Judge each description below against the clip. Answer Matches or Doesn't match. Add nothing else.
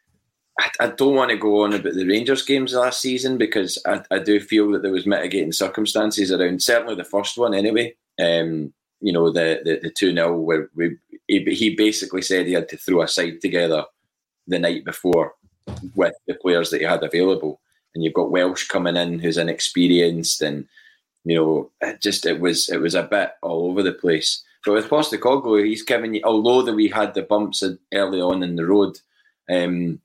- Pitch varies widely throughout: Doesn't match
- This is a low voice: Matches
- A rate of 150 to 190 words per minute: Doesn't match